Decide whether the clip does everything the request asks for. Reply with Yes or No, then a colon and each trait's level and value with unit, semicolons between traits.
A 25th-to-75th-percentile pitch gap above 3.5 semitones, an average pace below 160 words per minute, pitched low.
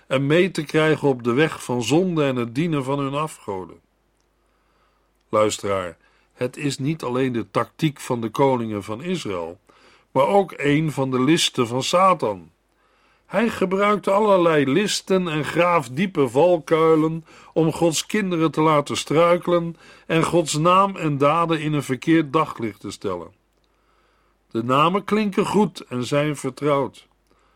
No: average, 4.3 semitones; average, 145 wpm; medium, 155 Hz